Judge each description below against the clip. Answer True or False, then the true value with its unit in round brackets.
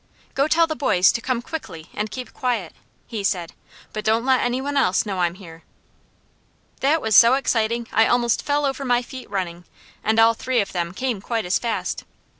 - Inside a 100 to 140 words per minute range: False (200 wpm)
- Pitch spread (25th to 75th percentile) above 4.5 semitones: True (4.9 semitones)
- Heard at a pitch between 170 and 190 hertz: False (230 Hz)